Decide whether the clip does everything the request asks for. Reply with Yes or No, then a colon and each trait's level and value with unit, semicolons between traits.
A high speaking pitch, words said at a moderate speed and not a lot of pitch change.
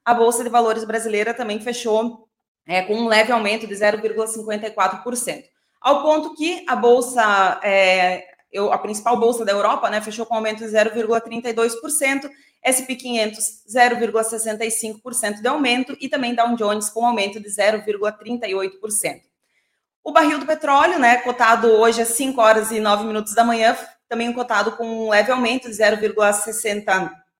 Yes: high, 225 Hz; average, 150 wpm; narrow, 2.3 semitones